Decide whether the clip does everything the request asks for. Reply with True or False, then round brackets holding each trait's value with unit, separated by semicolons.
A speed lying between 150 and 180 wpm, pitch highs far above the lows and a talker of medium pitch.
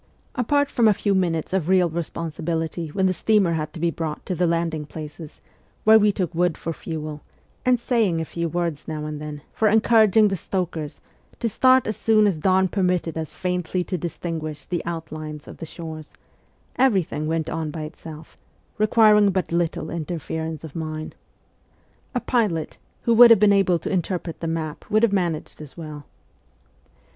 False (175 wpm; 3.9 semitones; 170 Hz)